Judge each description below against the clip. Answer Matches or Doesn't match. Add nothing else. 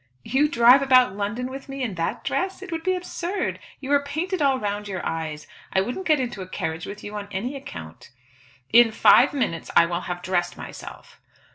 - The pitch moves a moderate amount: Doesn't match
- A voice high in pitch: Matches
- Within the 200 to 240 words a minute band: Matches